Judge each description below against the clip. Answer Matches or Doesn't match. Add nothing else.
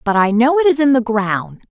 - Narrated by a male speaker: Doesn't match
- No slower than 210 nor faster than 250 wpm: Doesn't match